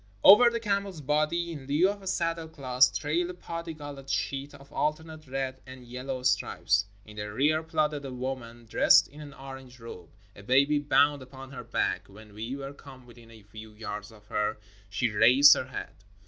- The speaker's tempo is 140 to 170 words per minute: No, average, 190 wpm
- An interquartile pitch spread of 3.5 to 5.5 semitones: Yes, average, 4.2 semitones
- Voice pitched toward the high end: No, low, 135 Hz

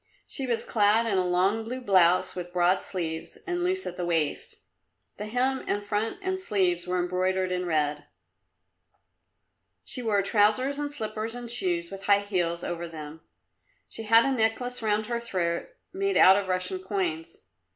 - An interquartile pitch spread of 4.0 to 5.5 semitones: Yes, average, 4.4 semitones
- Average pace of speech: Yes, average, 170 wpm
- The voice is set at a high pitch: Yes, high, 200 Hz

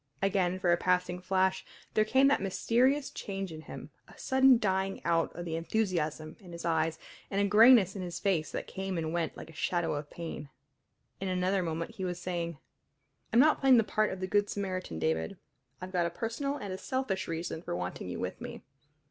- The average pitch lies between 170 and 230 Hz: Yes, medium, 185 Hz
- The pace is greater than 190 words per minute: Yes, fast, 205 wpm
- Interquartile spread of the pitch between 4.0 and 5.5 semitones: No, average, 3.3 semitones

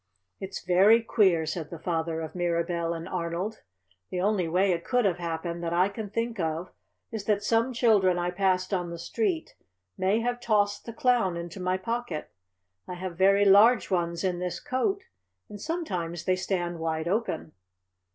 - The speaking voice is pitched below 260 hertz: Yes, medium, 185 Hz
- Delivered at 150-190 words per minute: Yes, average, 175 wpm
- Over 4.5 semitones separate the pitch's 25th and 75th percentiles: No, average, 4.0 semitones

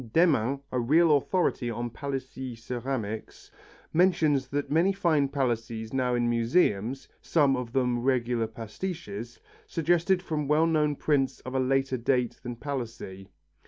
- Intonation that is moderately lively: Yes, average, 4.1 semitones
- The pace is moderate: No, slow, 130 wpm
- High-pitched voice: No, low, 130 Hz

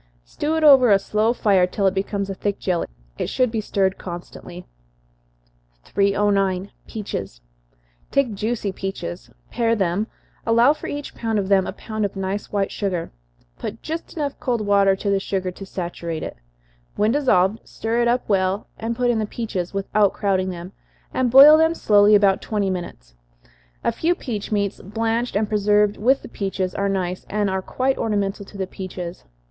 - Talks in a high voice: Yes, high, 200 Hz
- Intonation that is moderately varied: Yes, average, 3.0 semitones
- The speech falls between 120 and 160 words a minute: No, average, 175 wpm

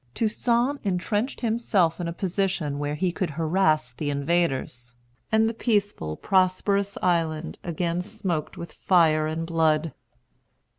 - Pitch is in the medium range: Yes, medium, 175 Hz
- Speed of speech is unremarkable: No, slow, 130 wpm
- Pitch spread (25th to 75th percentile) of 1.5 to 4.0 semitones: No, average, 4.4 semitones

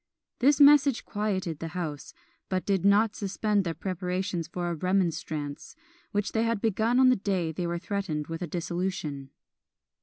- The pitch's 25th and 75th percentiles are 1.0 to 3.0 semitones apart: No, average, 3.7 semitones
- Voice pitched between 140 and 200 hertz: Yes, medium, 185 Hz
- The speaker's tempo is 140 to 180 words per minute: Yes, average, 160 wpm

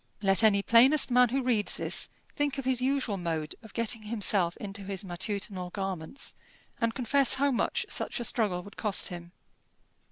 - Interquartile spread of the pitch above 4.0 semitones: Yes, average, 4.5 semitones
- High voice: Yes, high, 215 Hz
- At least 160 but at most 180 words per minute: Yes, average, 170 wpm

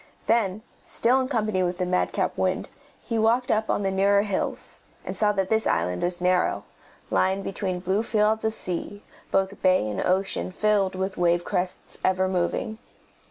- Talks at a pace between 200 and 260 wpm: No, average, 170 wpm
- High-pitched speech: Yes, high, 195 Hz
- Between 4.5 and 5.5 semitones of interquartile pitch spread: No, average, 2.8 semitones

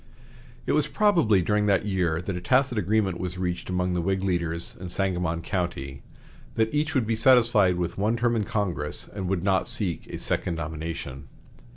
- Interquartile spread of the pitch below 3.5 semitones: No, average, 4.0 semitones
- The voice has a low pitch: Yes, very low, 95 Hz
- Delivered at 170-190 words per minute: Yes, average, 185 wpm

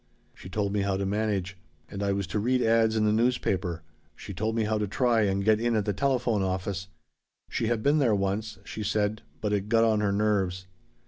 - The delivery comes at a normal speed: No, fast, 220 wpm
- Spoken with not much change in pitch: Yes, narrow, 2.3 semitones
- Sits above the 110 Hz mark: No, low, 105 Hz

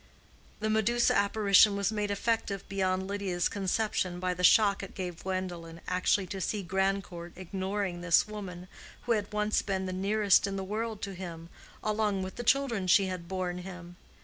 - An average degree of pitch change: No, narrow, 2.3 semitones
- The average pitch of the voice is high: Yes, high, 195 Hz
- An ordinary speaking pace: Yes, average, 175 wpm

